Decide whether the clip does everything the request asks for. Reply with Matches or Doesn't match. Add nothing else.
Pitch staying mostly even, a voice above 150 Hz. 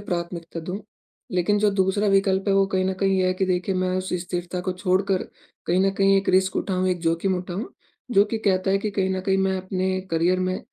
Matches